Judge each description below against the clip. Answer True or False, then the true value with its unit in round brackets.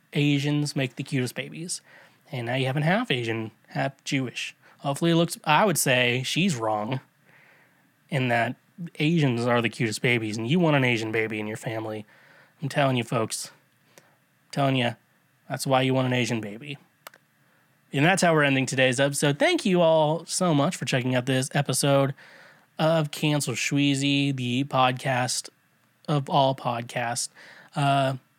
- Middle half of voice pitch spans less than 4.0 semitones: True (3.2 semitones)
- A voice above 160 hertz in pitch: False (140 Hz)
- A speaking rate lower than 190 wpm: True (165 wpm)